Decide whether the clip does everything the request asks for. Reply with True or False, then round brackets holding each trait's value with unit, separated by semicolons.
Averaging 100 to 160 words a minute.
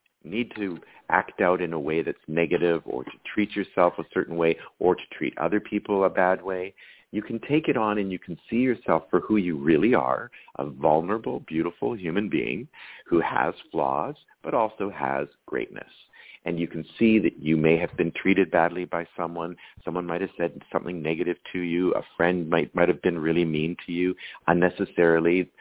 False (195 wpm)